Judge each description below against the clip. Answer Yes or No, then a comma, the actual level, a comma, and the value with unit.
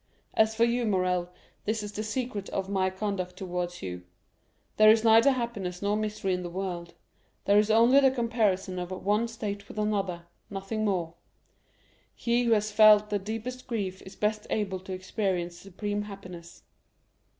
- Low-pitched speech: No, high, 205 Hz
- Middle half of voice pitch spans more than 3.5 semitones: No, average, 2.8 semitones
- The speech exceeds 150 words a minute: Yes, average, 165 wpm